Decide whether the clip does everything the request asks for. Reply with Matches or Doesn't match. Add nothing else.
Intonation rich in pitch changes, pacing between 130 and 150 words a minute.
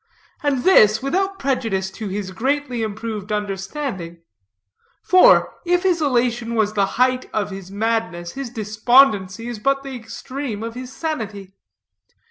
Doesn't match